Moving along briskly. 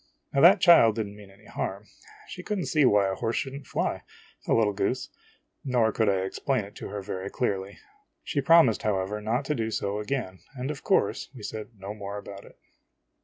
Yes: fast, 215 wpm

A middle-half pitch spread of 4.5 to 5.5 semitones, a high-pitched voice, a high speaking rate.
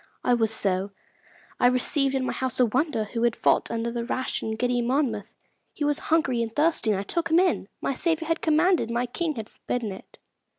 Yes: average, 5.0 semitones; high, 245 Hz; fast, 215 wpm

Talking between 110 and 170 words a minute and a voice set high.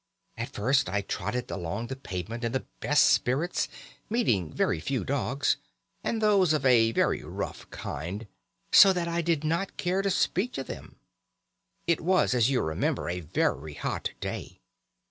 No: average, 165 wpm; low, 130 Hz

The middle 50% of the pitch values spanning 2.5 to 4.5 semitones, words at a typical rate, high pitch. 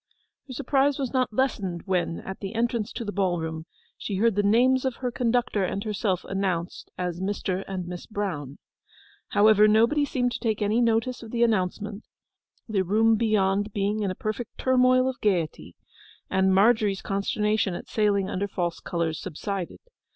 Yes: average, 3.5 semitones; average, 165 wpm; high, 210 Hz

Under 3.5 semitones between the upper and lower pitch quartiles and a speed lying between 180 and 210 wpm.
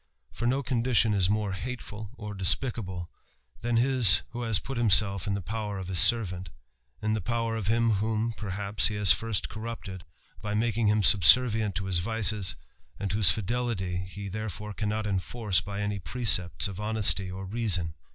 No: average, 2.9 semitones; average, 170 wpm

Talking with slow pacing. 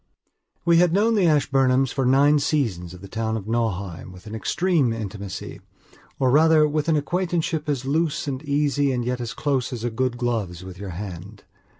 No: average, 185 wpm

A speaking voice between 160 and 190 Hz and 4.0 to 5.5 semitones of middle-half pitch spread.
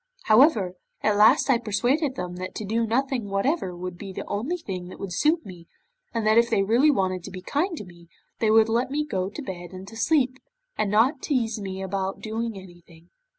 No: high, 215 Hz; average, 5.2 semitones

